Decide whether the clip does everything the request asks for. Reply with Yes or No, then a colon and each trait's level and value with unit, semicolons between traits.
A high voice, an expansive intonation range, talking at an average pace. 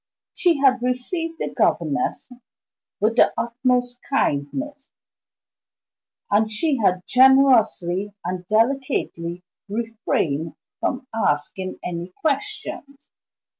No: high, 230 Hz; wide, 6.4 semitones; slow, 90 wpm